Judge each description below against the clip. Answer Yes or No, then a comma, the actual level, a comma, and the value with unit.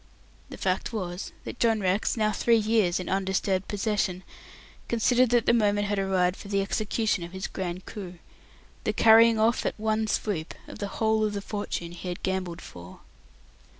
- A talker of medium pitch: No, high, 200 Hz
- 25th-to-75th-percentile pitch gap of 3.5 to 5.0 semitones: No, average, 2.9 semitones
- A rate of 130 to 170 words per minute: No, average, 180 wpm